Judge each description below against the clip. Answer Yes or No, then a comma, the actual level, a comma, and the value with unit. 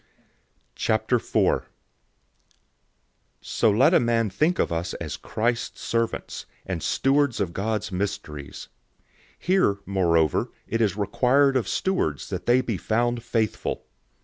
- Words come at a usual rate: No, slow, 120 wpm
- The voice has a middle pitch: No, low, 110 Hz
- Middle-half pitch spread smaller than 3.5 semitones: No, average, 4.1 semitones